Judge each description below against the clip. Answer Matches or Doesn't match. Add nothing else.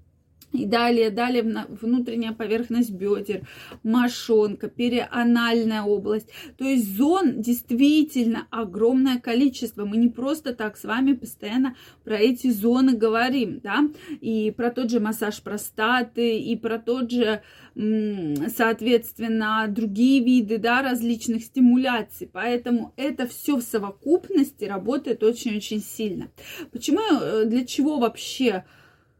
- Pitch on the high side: Matches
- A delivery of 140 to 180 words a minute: Doesn't match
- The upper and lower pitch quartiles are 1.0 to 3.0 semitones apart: Matches